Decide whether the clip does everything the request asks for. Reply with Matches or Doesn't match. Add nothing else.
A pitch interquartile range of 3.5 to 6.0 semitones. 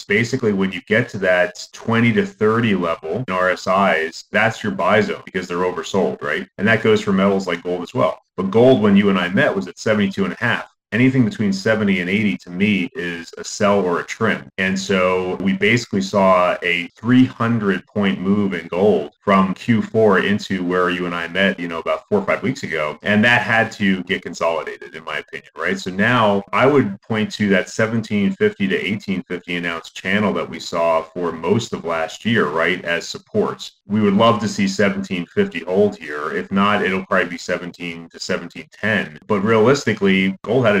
Matches